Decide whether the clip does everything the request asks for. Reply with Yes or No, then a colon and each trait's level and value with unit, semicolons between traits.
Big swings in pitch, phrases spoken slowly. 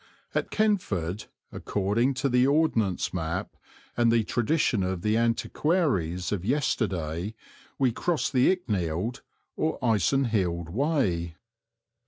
Yes: wide, 6.9 semitones; slow, 110 wpm